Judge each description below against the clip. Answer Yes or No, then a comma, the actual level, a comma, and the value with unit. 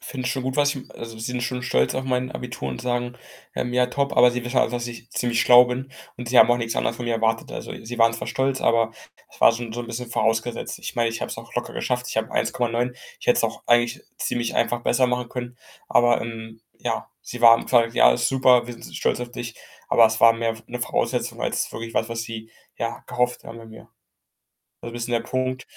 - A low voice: Yes, low, 120 Hz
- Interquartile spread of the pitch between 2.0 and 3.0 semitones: No, narrow, 1.3 semitones